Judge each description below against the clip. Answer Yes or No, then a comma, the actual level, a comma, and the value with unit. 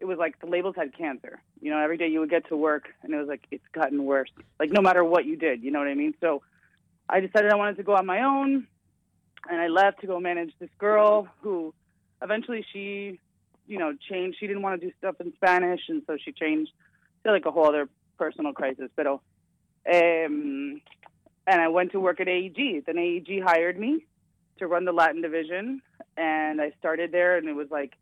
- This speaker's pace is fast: Yes, fast, 220 wpm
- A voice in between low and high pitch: Yes, medium, 175 Hz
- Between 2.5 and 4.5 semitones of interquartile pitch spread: Yes, average, 4.1 semitones